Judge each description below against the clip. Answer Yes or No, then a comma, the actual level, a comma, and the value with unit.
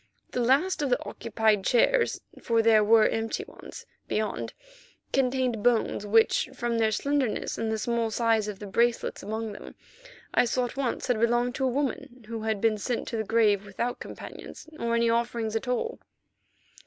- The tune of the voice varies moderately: No, narrow, 2.1 semitones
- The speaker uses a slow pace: No, average, 180 wpm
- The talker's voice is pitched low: No, high, 230 Hz